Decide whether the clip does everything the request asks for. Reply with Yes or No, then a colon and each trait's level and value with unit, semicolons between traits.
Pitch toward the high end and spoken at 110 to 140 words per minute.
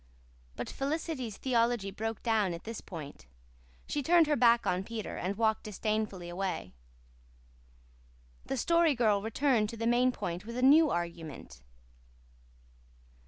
Yes: high, 225 Hz; slow, 135 wpm